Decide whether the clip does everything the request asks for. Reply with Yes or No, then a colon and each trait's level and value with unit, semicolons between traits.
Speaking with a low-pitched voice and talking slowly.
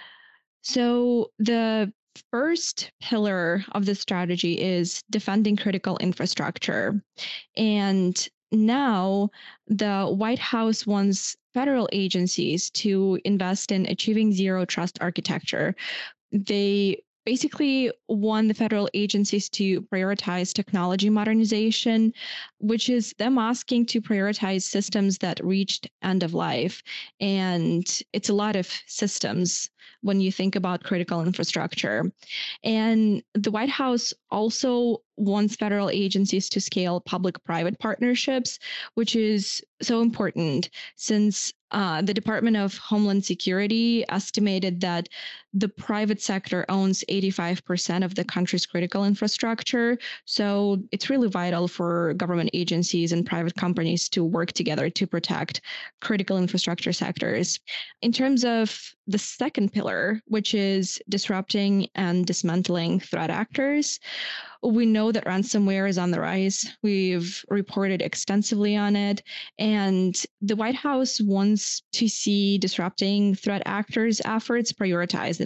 No: high, 200 Hz; slow, 120 wpm